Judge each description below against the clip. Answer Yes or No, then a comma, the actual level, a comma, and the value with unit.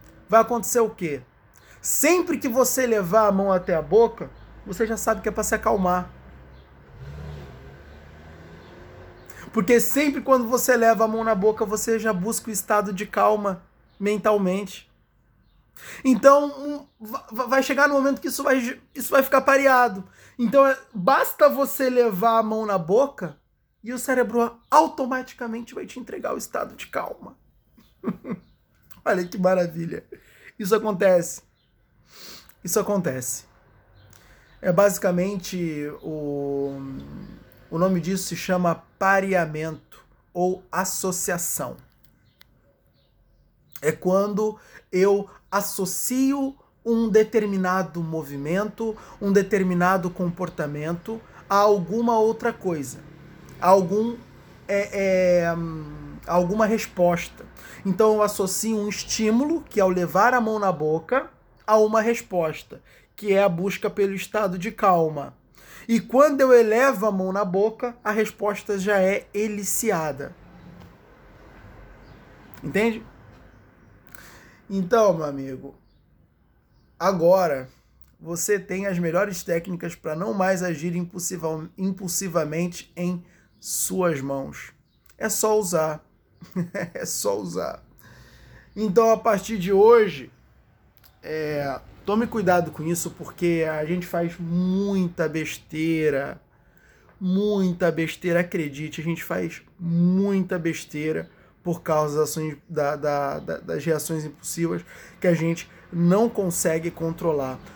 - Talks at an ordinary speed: No, slow, 115 wpm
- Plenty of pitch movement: No, average, 5.0 semitones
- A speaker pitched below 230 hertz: Yes, high, 190 Hz